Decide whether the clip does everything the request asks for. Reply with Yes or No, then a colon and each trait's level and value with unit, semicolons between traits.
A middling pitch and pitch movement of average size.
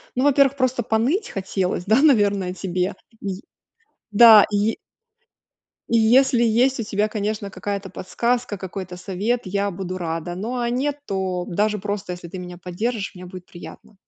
No: high, 205 Hz; average, 4.2 semitones